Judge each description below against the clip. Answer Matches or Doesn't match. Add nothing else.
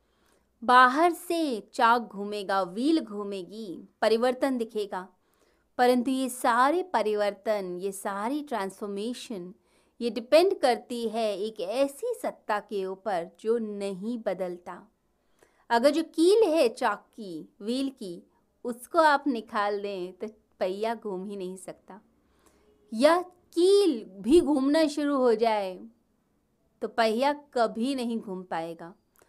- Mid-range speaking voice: Doesn't match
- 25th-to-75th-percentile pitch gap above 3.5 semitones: Matches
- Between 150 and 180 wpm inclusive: Doesn't match